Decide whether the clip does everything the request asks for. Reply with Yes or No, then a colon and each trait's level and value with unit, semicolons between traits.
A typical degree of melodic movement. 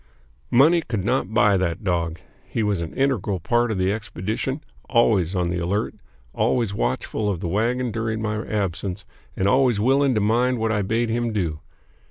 Yes: average, 4.1 semitones